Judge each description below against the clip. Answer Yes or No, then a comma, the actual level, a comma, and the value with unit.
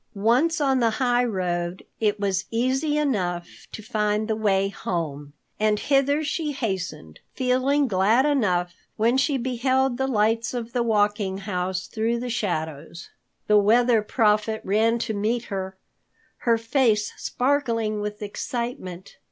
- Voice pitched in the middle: No, high, 220 Hz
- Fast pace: No, slow, 135 wpm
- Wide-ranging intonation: No, average, 4.1 semitones